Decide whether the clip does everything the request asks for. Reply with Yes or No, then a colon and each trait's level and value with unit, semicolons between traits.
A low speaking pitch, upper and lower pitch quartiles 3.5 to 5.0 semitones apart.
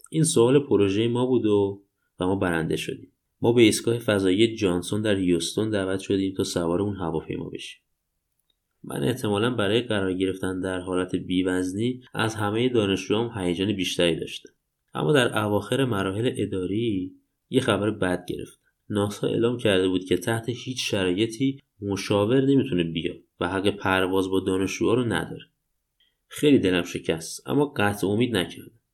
Yes: low, 100 Hz; average, 3.9 semitones